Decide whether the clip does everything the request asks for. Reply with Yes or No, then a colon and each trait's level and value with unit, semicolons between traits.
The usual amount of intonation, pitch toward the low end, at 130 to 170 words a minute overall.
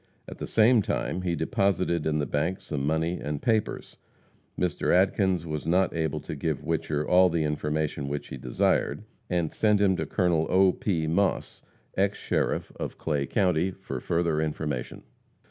Yes: average, 3.6 semitones; very low, 85 Hz; average, 165 wpm